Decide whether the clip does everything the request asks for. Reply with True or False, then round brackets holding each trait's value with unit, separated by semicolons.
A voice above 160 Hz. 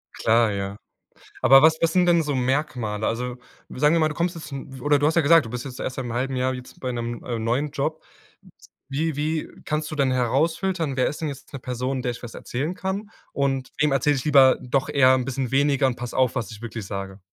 False (135 Hz)